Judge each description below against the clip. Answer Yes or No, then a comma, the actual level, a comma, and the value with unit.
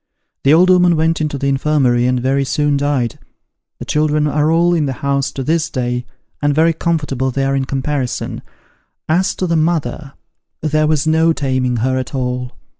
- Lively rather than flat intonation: No, average, 3.1 semitones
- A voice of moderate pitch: Yes, medium, 145 Hz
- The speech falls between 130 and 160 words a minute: No, average, 185 wpm